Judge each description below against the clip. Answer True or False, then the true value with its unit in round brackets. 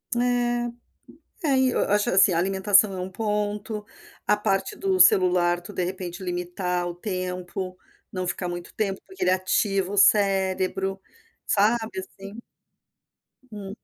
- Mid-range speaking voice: False (195 Hz)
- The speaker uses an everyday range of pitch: False (2.3 semitones)